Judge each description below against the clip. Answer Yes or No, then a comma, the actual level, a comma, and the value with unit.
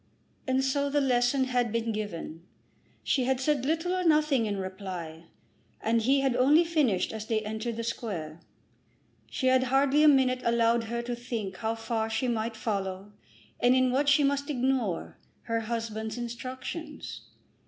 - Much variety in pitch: No, average, 3.4 semitones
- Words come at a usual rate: Yes, average, 165 wpm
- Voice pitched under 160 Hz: No, high, 240 Hz